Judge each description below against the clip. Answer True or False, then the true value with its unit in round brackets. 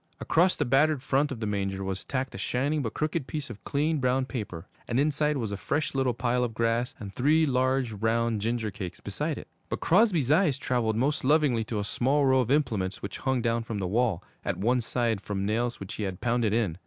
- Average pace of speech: False (225 wpm)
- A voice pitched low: True (120 Hz)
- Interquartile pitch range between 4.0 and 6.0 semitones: True (4.4 semitones)